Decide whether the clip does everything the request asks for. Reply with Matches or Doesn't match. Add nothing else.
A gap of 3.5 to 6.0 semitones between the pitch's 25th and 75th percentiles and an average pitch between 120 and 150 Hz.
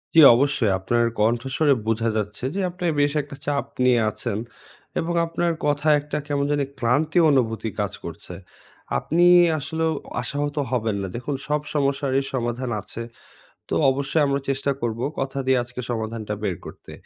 Matches